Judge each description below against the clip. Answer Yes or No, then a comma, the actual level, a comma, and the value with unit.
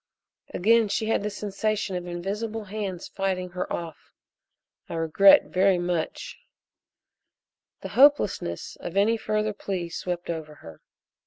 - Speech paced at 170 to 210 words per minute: No, slow, 135 wpm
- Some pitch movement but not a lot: Yes, average, 3.4 semitones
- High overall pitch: Yes, high, 195 Hz